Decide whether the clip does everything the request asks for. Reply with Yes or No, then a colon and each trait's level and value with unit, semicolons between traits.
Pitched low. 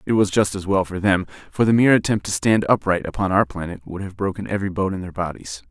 Yes: very low, 95 Hz